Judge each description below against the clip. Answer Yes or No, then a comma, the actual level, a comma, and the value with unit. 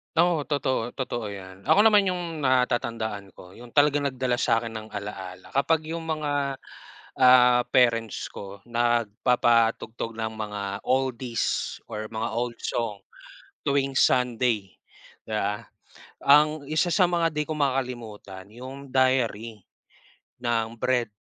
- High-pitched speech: No, low, 120 Hz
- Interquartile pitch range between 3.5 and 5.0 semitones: Yes, average, 3.9 semitones